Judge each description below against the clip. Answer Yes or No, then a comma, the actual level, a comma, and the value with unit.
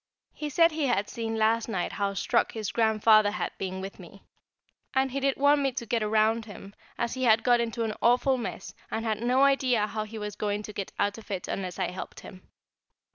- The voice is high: Yes, high, 225 Hz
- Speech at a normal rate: No, fast, 230 wpm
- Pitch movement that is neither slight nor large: Yes, average, 3.2 semitones